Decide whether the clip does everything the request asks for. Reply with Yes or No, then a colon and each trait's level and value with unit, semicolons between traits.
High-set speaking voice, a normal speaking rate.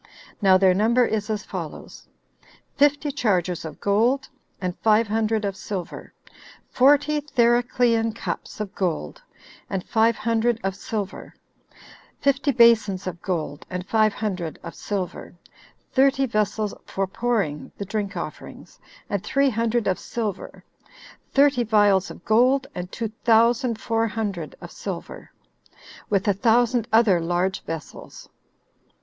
No: high, 215 Hz; slow, 130 wpm